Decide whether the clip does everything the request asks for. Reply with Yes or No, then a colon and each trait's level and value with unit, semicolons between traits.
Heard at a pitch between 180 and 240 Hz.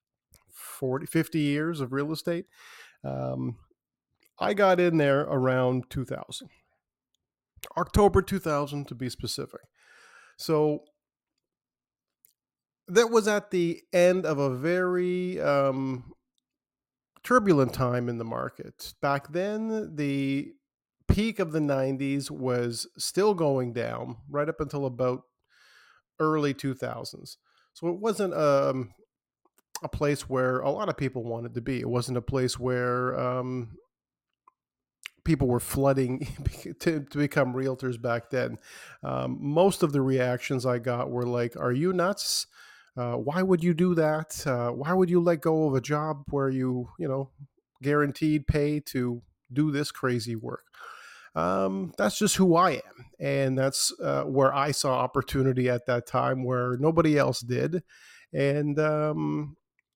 No: medium, 140 Hz